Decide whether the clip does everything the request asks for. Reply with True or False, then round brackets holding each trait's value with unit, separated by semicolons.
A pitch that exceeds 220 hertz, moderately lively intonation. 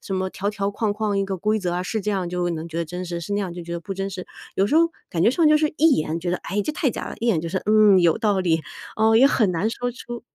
False (195 Hz; 3.8 semitones)